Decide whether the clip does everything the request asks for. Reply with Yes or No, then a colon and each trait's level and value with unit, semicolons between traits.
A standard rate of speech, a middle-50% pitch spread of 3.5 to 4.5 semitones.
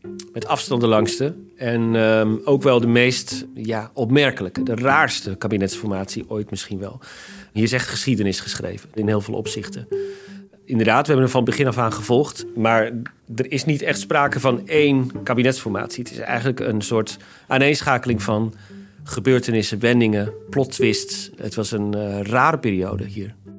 Yes: average, 160 wpm; average, 3.8 semitones